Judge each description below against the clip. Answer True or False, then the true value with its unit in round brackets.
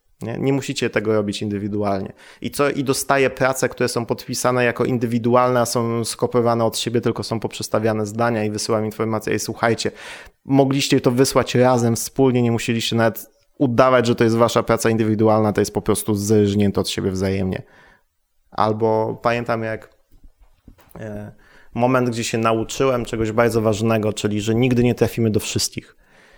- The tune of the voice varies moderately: False (2.2 semitones)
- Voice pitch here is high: False (115 Hz)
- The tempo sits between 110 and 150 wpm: False (160 wpm)